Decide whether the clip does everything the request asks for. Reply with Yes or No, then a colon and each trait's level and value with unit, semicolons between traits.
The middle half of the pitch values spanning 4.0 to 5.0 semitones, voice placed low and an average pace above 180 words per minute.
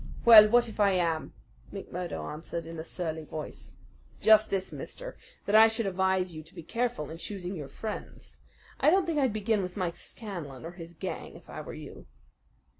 No: average, 4.7 semitones; high, 190 Hz; average, 190 wpm